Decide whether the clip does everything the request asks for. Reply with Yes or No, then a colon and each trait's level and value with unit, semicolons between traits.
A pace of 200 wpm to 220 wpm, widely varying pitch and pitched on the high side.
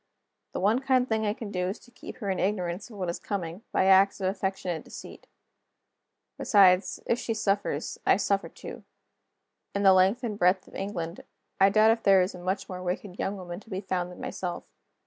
No: fast, 205 wpm; narrow, 2.4 semitones; high, 195 Hz